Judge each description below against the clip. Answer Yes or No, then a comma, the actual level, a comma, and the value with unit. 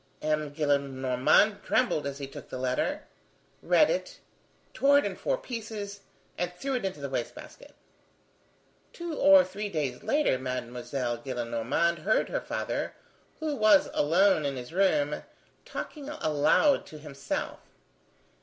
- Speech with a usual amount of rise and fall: No, wide, 7.9 semitones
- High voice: No, medium, 155 Hz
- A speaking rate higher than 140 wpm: No, slow, 135 wpm